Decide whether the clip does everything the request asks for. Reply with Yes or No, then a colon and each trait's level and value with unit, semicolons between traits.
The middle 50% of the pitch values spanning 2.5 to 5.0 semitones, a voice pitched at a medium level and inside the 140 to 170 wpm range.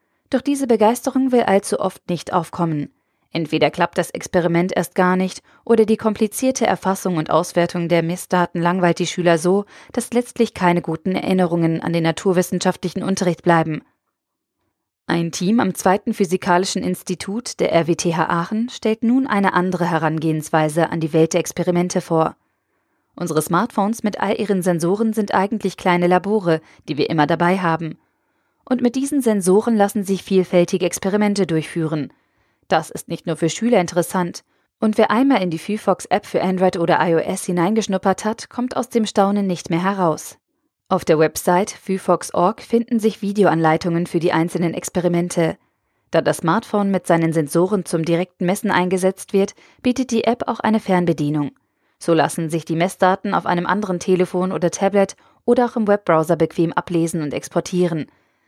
Yes: average, 3.3 semitones; medium, 180 Hz; average, 160 wpm